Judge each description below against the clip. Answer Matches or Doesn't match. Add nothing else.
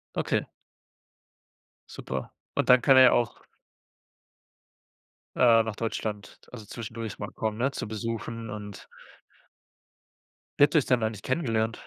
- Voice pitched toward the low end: Matches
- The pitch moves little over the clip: Matches